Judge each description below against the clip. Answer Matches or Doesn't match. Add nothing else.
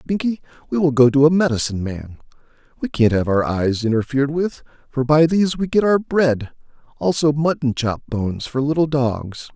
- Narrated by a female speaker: Doesn't match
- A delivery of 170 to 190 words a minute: Matches